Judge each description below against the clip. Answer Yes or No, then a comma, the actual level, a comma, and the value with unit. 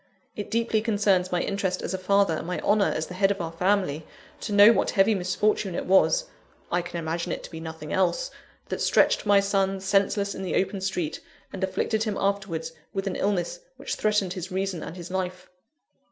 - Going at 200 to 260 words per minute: Yes, fast, 205 wpm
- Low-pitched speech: No, high, 195 Hz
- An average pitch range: No, narrow, 2.1 semitones